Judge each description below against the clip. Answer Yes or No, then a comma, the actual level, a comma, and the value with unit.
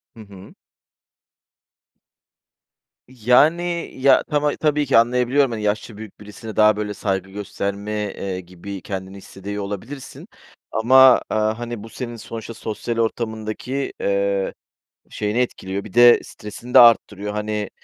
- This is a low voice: Yes, low, 110 Hz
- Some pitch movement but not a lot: Yes, average, 3.2 semitones